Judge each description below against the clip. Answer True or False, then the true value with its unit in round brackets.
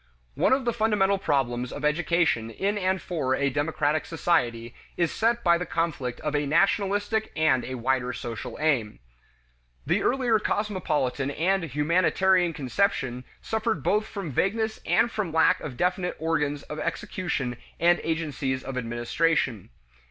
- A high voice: False (160 Hz)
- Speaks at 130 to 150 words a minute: True (145 wpm)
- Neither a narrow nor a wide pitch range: False (6.5 semitones)